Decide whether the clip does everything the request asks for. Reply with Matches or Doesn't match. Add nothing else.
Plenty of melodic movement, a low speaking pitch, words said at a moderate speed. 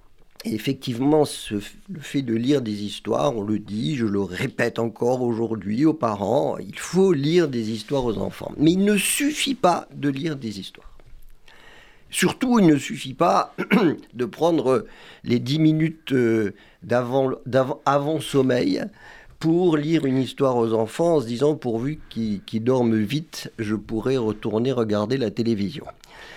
Matches